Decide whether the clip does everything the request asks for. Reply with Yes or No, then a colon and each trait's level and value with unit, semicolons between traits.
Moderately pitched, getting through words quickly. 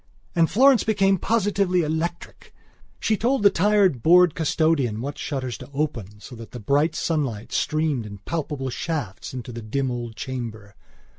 No: medium, 150 Hz; average, 155 wpm